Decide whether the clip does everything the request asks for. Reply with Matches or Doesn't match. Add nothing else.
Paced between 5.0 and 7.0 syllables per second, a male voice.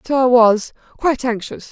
Doesn't match